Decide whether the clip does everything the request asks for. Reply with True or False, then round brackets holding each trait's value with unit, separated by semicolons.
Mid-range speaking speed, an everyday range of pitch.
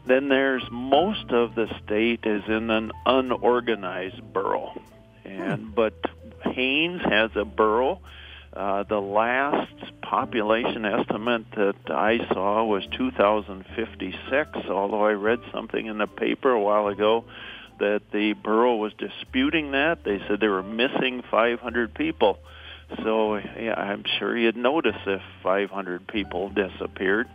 False (130 wpm; 3.3 semitones)